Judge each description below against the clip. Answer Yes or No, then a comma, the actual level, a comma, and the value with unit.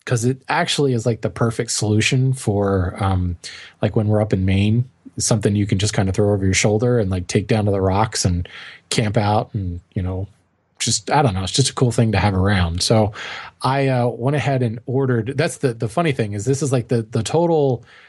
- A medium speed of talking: No, fast, 230 wpm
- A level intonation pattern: No, average, 3.9 semitones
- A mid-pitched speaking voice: No, low, 115 Hz